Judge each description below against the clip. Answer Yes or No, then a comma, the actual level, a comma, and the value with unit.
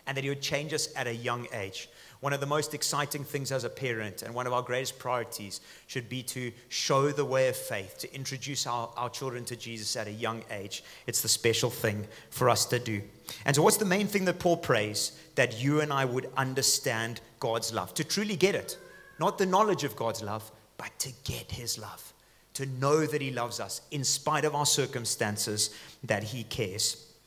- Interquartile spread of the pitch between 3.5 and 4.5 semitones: Yes, average, 3.9 semitones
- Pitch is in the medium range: No, low, 125 Hz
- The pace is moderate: No, fast, 215 wpm